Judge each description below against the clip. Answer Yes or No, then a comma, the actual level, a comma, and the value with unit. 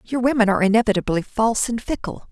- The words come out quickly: No, average, 180 wpm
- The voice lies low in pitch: No, high, 220 Hz